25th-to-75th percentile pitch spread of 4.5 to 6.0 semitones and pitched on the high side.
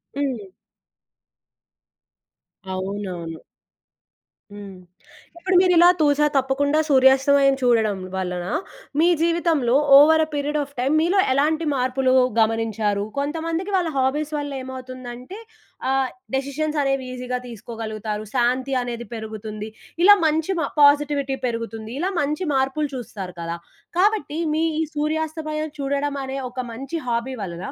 Yes: average, 4.8 semitones; very high, 270 Hz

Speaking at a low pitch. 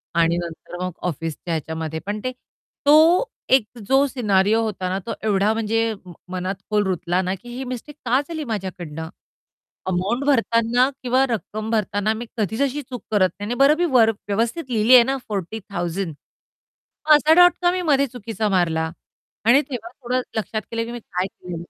No: high, 220 Hz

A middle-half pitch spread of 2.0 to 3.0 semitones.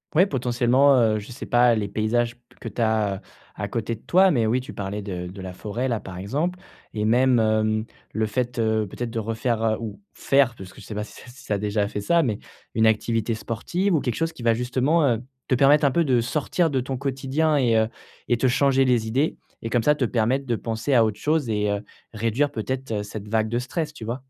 No: average, 3.5 semitones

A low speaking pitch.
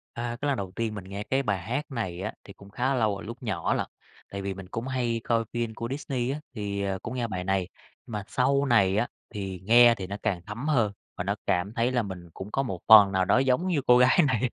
Yes: low, 115 Hz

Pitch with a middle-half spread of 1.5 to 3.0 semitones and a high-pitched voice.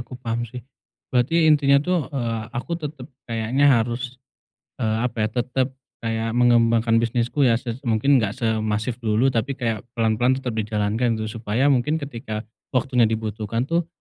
No: average, 2.7 semitones; low, 120 Hz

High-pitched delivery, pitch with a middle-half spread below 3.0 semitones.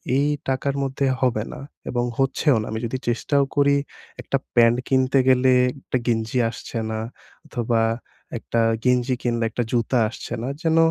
No: low, 125 Hz; narrow, 2.4 semitones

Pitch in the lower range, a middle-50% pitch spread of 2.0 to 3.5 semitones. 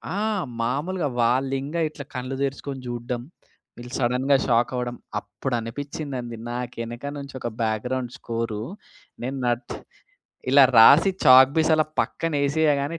Yes: low, 130 Hz; average, 2.9 semitones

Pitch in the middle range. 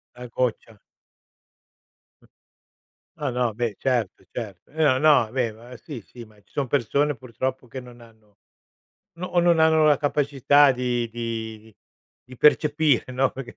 No: low, 125 Hz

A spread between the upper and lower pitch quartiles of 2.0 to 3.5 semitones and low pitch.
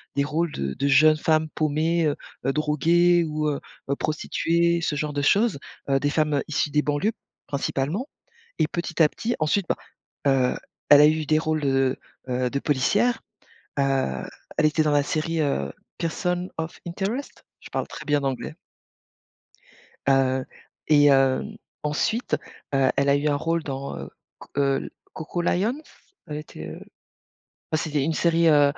No: average, 3.0 semitones; medium, 150 Hz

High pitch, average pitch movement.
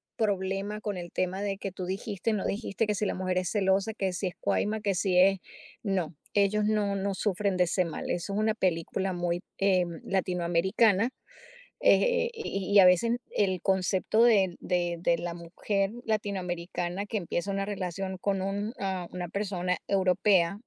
No: high, 195 Hz; narrow, 2.1 semitones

